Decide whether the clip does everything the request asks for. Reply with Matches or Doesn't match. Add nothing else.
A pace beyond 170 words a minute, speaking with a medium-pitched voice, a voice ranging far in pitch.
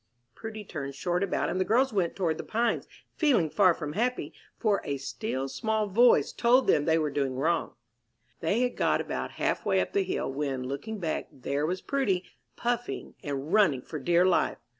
Matches